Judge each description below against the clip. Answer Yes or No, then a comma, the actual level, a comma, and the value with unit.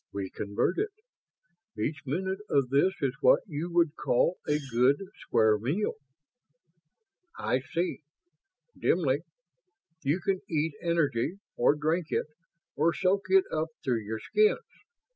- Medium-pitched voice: Yes, medium, 150 Hz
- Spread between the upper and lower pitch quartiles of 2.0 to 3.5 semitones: No, average, 5.3 semitones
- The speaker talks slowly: Yes, slow, 130 wpm